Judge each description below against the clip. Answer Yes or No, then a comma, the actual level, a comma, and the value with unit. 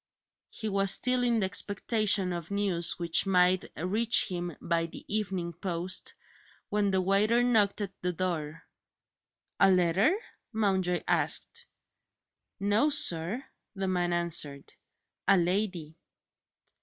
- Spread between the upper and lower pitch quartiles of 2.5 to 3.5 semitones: Yes, average, 2.9 semitones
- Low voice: No, high, 190 Hz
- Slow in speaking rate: Yes, slow, 120 wpm